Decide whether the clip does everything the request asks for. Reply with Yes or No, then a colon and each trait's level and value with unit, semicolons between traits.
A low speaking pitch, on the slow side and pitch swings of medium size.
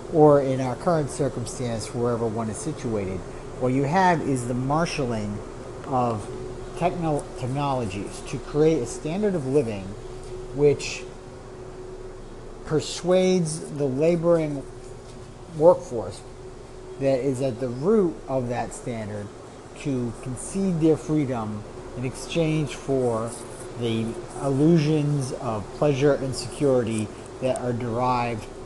Yes: low, 125 Hz; slow, 110 wpm; average, 3.5 semitones